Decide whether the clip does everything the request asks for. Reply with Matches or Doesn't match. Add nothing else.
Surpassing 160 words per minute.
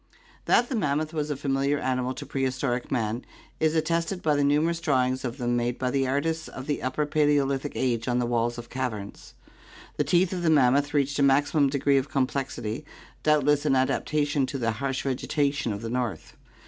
Matches